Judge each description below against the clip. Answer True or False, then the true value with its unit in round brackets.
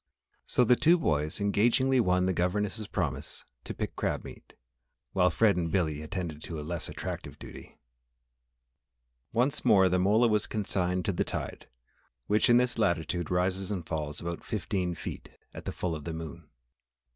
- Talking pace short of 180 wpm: True (170 wpm)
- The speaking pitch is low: True (90 Hz)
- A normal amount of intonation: True (4.1 semitones)